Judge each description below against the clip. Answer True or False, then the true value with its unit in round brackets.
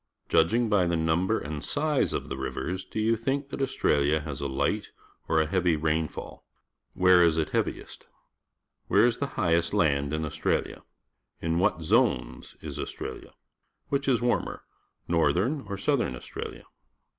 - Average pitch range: False (6.7 semitones)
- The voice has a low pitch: True (85 Hz)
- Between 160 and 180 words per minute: True (170 wpm)